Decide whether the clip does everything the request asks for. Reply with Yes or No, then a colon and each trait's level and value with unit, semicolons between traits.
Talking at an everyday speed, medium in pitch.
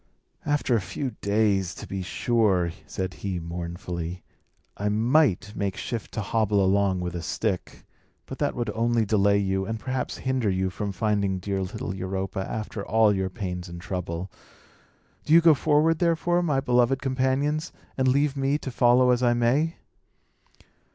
No: average, 165 wpm; low, 105 Hz